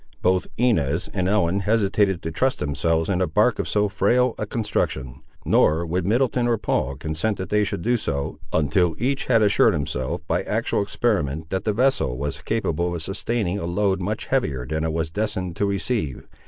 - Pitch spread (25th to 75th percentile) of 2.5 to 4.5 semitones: No, average, 5.1 semitones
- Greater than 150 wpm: Yes, average, 190 wpm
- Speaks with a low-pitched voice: Yes, very low, 95 Hz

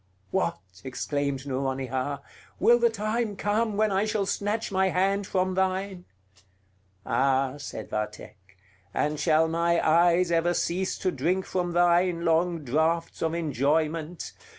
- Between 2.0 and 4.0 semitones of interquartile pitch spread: No, average, 4.8 semitones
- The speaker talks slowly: Yes, slow, 130 wpm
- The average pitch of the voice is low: No, medium, 170 Hz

